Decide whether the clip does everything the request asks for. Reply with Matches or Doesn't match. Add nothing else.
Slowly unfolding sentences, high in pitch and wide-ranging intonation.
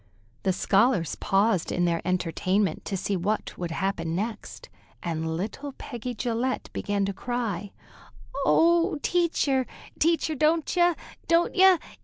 Matches